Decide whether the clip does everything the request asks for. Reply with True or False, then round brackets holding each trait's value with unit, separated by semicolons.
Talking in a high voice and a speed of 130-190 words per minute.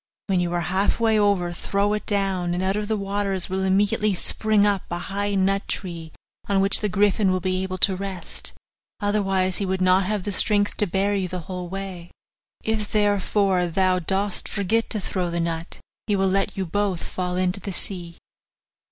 False (195 Hz; 200 wpm)